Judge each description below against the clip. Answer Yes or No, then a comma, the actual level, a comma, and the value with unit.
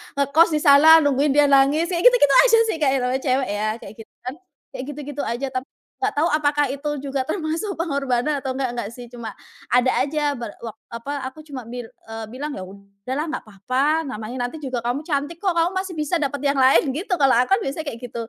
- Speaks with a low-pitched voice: No, very high, 280 Hz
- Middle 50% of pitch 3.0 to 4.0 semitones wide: Yes, average, 3.6 semitones